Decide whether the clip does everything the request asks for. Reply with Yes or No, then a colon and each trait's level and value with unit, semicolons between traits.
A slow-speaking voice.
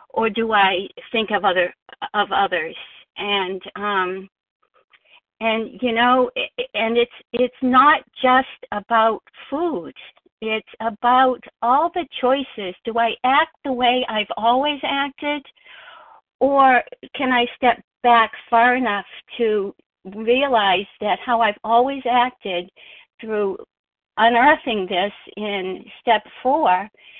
Yes: slow, 115 wpm